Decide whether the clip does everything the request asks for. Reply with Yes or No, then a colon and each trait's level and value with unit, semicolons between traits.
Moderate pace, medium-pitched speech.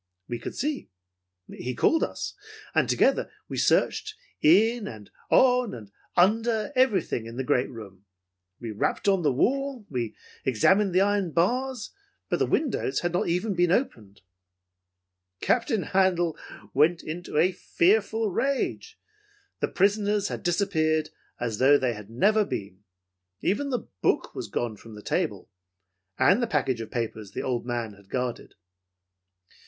Yes: average, 150 wpm; medium, 175 Hz